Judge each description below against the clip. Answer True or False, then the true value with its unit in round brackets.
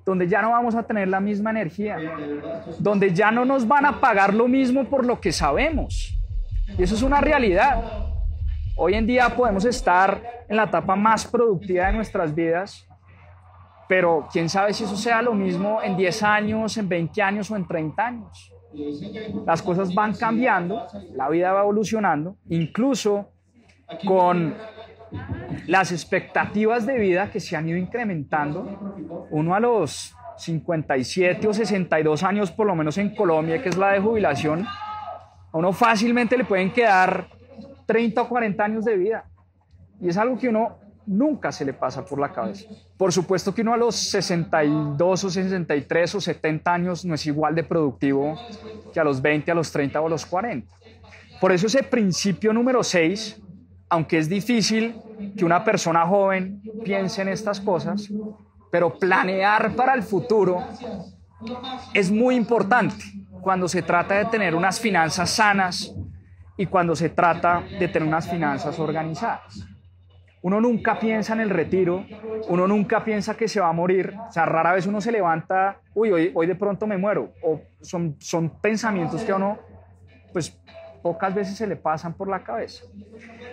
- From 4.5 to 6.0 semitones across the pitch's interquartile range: True (5.1 semitones)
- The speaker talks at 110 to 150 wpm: False (165 wpm)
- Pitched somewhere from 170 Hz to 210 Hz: True (190 Hz)